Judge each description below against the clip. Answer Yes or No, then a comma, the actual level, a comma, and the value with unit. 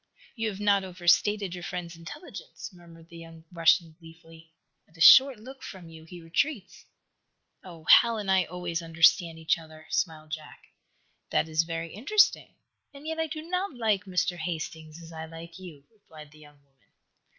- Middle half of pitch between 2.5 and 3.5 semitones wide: No, average, 4.0 semitones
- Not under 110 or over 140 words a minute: No, average, 175 wpm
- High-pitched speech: No, medium, 170 Hz